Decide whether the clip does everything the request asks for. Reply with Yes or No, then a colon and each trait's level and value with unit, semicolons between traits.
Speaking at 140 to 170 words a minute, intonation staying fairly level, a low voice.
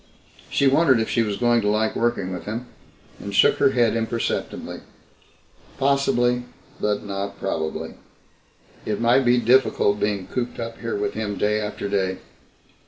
No: average, 155 wpm; average, 3.0 semitones; low, 110 Hz